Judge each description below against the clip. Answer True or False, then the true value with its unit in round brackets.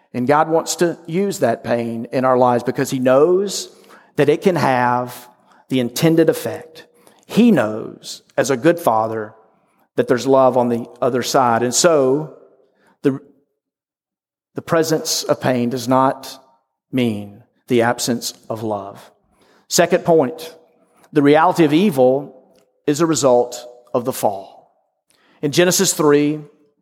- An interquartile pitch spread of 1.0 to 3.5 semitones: False (4.3 semitones)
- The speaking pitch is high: False (135 Hz)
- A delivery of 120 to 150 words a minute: True (140 wpm)